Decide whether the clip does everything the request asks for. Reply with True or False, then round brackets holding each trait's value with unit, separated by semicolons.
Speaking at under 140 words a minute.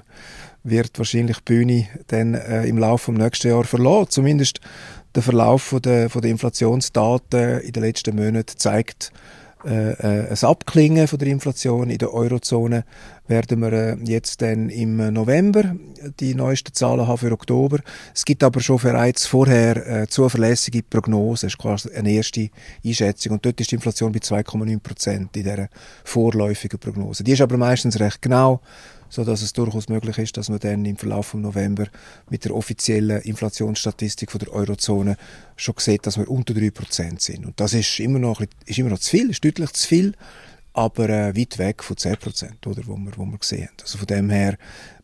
False (185 wpm)